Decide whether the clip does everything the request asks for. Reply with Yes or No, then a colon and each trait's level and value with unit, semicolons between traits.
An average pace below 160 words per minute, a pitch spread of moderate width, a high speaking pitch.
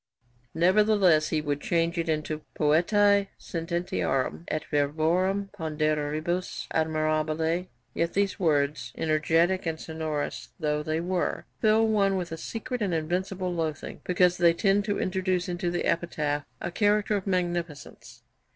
No: slow, 135 wpm; average, 3.2 semitones; medium, 170 Hz